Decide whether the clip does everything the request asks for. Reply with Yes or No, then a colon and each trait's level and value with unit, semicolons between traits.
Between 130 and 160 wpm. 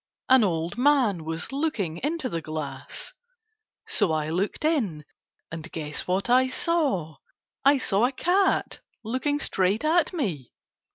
Yes: slow, 135 wpm